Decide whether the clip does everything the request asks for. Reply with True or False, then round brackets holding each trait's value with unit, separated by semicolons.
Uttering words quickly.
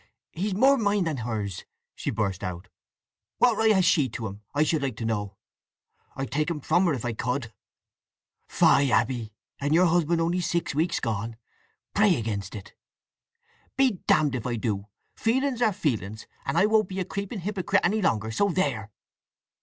False (170 wpm)